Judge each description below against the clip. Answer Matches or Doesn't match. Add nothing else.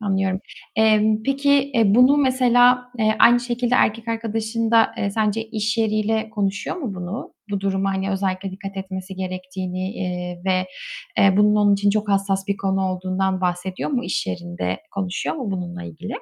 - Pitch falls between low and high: Doesn't match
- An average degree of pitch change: Matches